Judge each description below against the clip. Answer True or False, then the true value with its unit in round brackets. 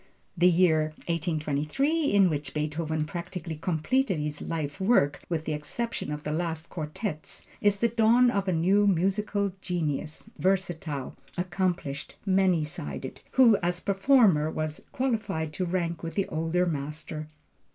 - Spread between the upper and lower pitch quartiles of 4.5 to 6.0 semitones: False (4.1 semitones)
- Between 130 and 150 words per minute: True (140 wpm)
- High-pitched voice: False (170 Hz)